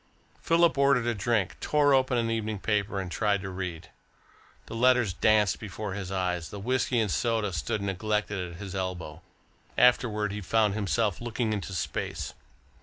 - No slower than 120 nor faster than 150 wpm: No, average, 165 wpm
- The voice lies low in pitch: Yes, low, 105 Hz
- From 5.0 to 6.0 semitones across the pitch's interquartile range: No, average, 3.4 semitones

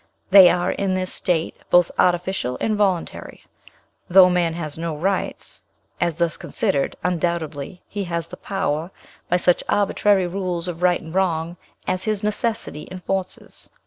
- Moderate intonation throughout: No, narrow, 2.2 semitones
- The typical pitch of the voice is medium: Yes, medium, 180 Hz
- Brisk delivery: No, average, 145 wpm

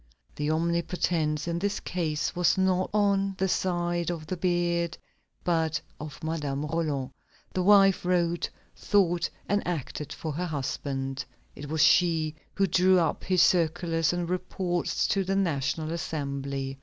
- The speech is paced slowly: No, average, 145 wpm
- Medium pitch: Yes, medium, 170 Hz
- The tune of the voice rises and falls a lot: No, average, 2.9 semitones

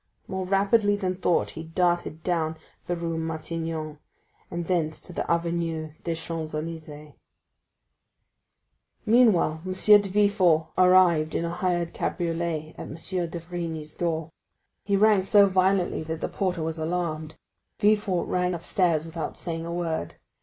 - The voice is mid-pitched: Yes, medium, 170 Hz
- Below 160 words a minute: Yes, average, 140 wpm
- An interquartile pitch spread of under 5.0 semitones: Yes, narrow, 2.4 semitones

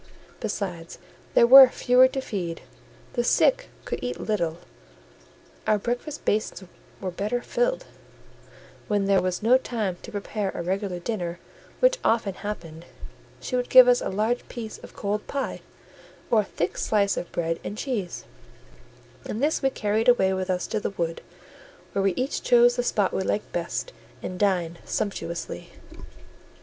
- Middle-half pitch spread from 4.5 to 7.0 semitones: Yes, average, 4.8 semitones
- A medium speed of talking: Yes, average, 160 wpm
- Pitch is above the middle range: Yes, high, 210 Hz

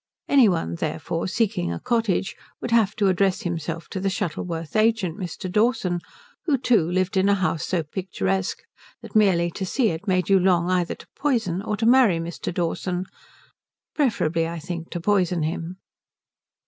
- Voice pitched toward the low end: No, medium, 185 Hz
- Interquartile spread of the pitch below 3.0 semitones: No, average, 3.8 semitones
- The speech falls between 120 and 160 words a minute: No, average, 170 wpm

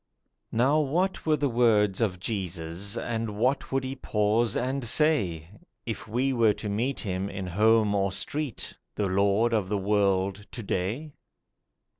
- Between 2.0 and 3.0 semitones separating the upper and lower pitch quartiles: No, average, 4.3 semitones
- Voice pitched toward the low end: Yes, low, 105 Hz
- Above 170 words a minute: No, average, 150 wpm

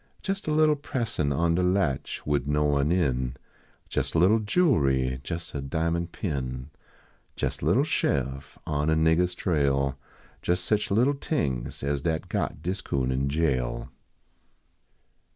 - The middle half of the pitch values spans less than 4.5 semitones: No, average, 4.8 semitones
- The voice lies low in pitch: Yes, very low, 80 Hz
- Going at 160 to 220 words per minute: No, average, 150 wpm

